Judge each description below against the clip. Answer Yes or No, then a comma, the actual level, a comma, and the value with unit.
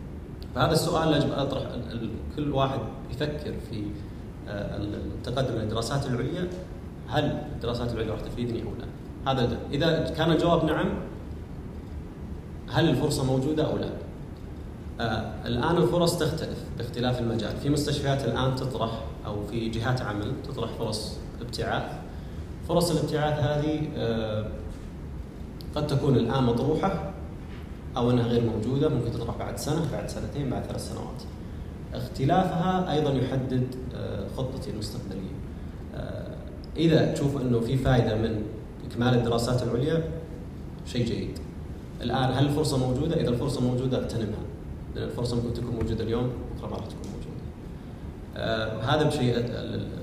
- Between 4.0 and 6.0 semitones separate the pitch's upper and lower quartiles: Yes, average, 5.1 semitones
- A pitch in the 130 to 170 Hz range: No, low, 120 Hz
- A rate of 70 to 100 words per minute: No, average, 125 wpm